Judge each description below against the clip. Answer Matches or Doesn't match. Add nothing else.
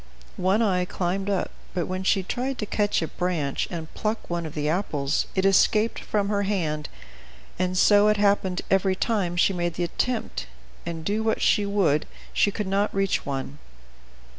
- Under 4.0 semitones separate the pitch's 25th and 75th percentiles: Matches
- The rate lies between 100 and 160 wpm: Doesn't match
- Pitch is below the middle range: Doesn't match